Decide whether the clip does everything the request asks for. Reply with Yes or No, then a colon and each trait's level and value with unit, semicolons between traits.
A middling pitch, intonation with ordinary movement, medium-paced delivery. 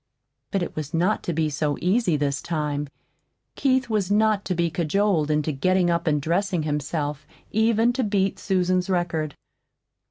Yes: medium, 175 Hz; average, 4.6 semitones; average, 160 wpm